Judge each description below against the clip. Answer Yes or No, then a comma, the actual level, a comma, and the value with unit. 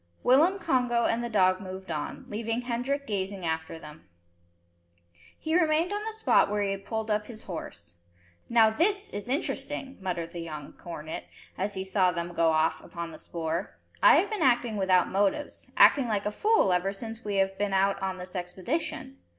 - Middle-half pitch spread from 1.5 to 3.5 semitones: No, wide, 5.5 semitones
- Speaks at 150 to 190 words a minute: Yes, average, 185 wpm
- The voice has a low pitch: No, high, 200 Hz